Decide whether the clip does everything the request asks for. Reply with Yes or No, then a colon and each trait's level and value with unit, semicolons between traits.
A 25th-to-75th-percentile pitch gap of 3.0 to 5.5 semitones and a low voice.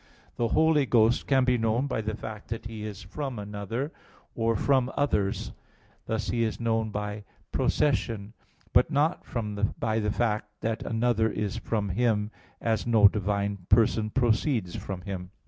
No: narrow, 2.5 semitones; low, 110 Hz